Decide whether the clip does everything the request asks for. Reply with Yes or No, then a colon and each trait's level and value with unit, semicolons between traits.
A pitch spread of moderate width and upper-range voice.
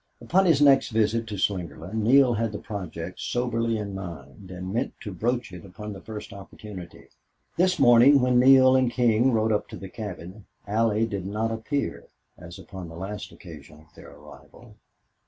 No: average, 4.6 semitones; low, 105 Hz